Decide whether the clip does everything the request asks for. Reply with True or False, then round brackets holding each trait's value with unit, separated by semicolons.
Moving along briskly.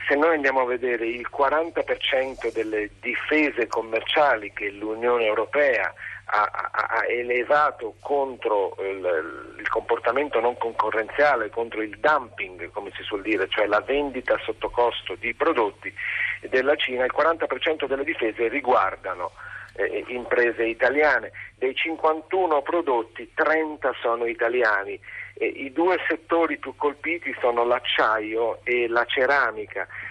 False (125 wpm)